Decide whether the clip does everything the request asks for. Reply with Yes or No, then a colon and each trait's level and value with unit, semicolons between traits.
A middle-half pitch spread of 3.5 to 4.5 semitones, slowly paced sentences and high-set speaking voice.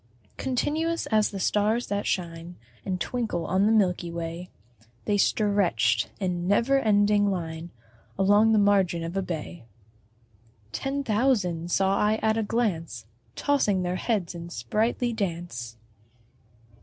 Yes: average, 4.0 semitones; slow, 130 wpm; high, 195 Hz